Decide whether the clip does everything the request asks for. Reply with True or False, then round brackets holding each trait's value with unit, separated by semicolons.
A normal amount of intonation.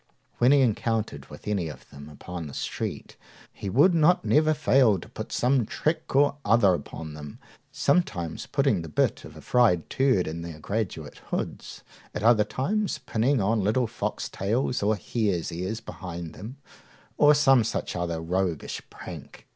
False (7.2 semitones)